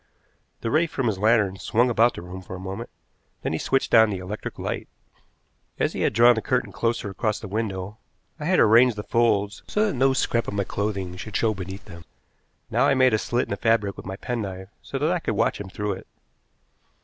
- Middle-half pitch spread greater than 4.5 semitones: No, average, 3.7 semitones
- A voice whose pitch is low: Yes, low, 110 Hz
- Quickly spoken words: Yes, fast, 225 wpm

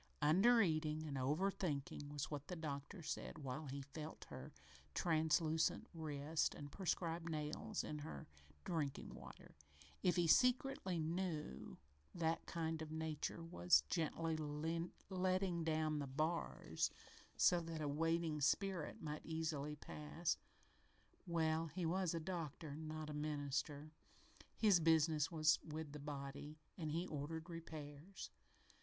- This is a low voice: No, medium, 155 Hz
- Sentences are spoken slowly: Yes, slow, 130 wpm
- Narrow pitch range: Yes, narrow, 2.1 semitones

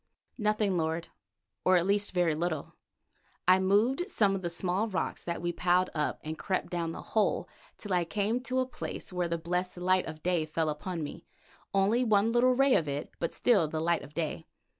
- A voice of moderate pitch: Yes, medium, 180 Hz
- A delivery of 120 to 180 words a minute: No, fast, 205 wpm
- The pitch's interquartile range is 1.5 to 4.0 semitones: Yes, average, 3.7 semitones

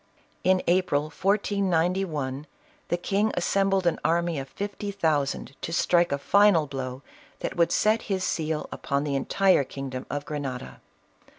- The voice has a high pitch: No, medium, 170 Hz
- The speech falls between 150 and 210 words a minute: No, average, 140 wpm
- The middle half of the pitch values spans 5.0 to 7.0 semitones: Yes, average, 5.3 semitones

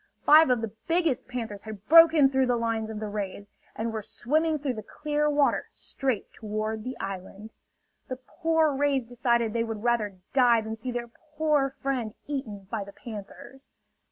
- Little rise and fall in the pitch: No, average, 4.2 semitones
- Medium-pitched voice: No, high, 240 Hz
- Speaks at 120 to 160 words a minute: No, average, 170 wpm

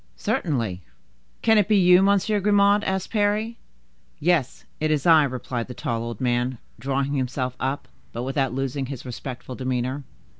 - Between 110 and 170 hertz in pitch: Yes, low, 135 Hz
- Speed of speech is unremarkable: Yes, average, 155 wpm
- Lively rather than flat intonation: Yes, wide, 7.1 semitones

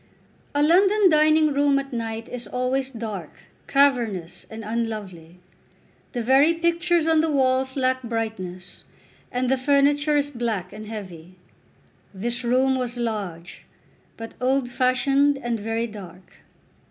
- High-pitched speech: Yes, very high, 250 Hz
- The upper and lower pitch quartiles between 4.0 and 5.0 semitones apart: Yes, average, 4.3 semitones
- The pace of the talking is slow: Yes, slow, 130 wpm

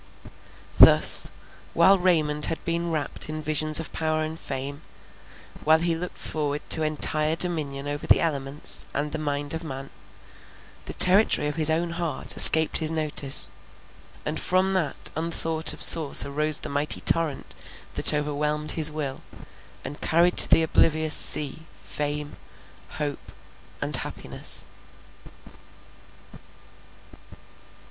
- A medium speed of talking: No, slow, 130 wpm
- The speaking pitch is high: No, medium, 155 Hz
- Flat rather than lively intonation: Yes, narrow, 1.8 semitones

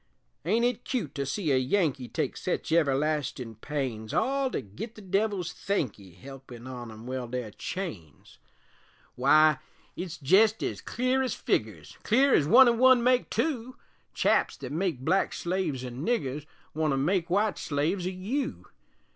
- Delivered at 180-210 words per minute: No, average, 160 wpm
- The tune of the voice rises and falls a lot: Yes, wide, 8.6 semitones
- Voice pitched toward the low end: No, medium, 160 Hz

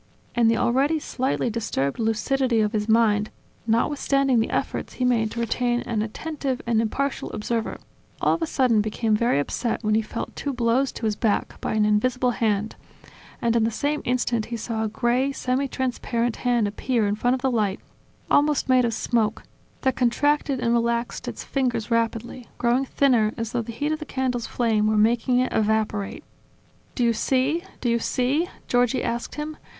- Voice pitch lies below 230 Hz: No, high, 235 Hz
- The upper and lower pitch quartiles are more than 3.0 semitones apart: No, average, 2.7 semitones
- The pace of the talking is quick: No, average, 185 wpm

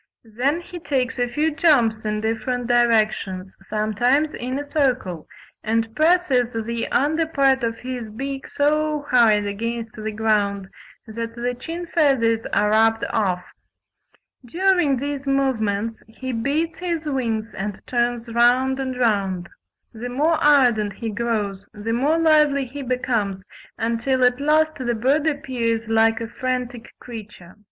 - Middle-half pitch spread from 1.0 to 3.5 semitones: No, average, 4.0 semitones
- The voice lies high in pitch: Yes, high, 240 Hz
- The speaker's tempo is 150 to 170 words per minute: No, average, 140 wpm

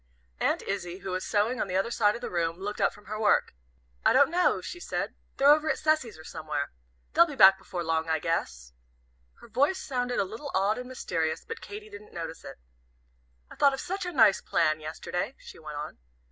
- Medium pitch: No, high, 205 Hz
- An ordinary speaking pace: No, fast, 215 wpm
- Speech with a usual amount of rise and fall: No, wide, 9.0 semitones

